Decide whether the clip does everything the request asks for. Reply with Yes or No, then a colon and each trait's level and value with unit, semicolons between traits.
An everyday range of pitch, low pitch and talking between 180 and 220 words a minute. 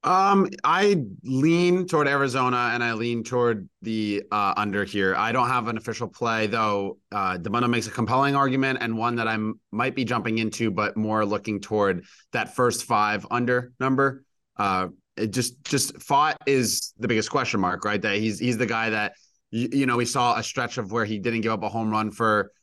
Yes: average, 3.1 semitones; low, 120 Hz; fast, 205 wpm